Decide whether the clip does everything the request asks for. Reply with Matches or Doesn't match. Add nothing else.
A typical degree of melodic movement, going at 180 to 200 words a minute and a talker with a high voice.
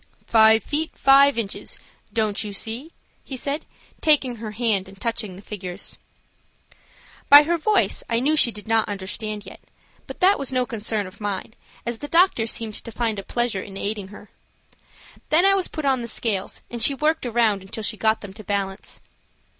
Matches